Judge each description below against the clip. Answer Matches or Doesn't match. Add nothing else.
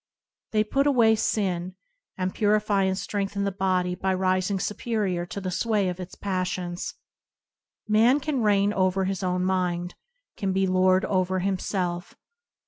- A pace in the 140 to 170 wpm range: Matches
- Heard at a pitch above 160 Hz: Matches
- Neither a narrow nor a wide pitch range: Doesn't match